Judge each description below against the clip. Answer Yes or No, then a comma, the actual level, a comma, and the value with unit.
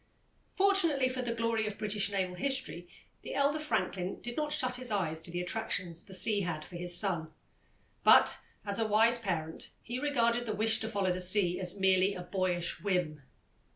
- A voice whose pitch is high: Yes, high, 200 Hz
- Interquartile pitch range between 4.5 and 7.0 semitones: Yes, average, 4.8 semitones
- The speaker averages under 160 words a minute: No, average, 190 wpm